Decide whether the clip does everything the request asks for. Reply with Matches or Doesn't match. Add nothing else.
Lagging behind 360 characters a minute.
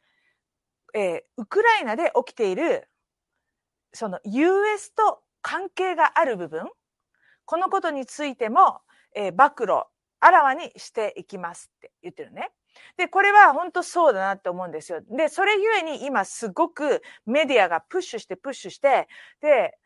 Matches